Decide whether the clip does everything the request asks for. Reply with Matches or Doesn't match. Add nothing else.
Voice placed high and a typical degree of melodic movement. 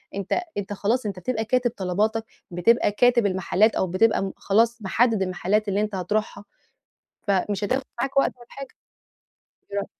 Matches